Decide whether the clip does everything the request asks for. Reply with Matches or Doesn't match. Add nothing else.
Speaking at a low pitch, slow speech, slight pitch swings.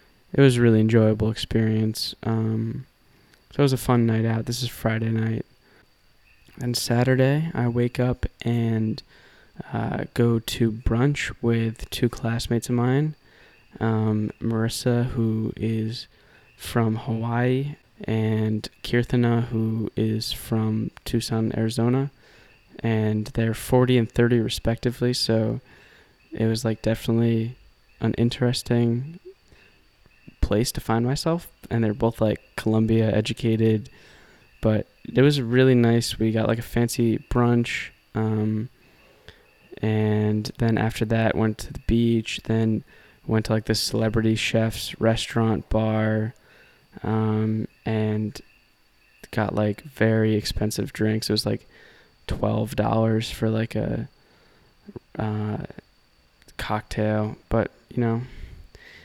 Matches